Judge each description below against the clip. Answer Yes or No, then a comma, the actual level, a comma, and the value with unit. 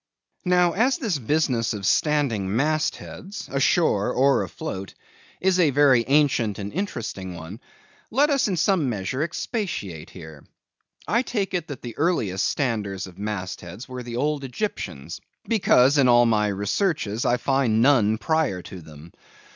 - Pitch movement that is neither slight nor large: No, wide, 7.9 semitones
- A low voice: Yes, low, 130 Hz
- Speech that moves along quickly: No, average, 155 wpm